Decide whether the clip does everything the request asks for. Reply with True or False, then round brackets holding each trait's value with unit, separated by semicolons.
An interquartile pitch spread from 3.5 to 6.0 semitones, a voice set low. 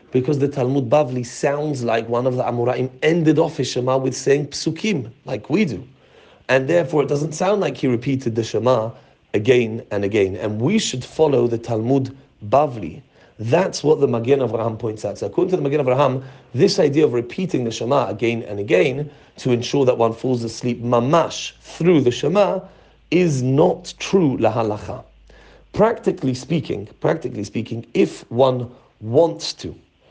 True (4.1 semitones; 130 Hz)